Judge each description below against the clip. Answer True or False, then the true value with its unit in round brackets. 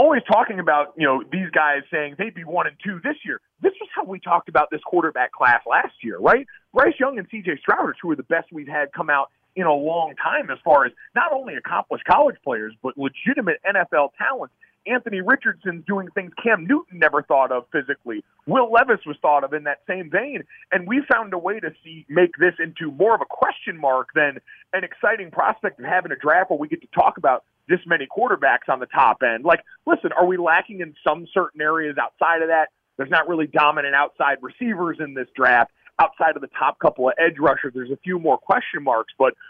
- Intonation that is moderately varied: False (6.6 semitones)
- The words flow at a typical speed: False (225 wpm)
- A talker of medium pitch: True (175 Hz)